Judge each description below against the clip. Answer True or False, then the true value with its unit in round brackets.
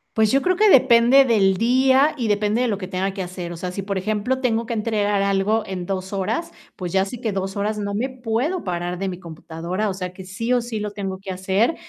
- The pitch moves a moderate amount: True (3.7 semitones)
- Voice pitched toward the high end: True (205 Hz)